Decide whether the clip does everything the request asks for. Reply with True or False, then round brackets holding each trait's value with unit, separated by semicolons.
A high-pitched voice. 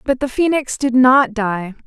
True (250 Hz)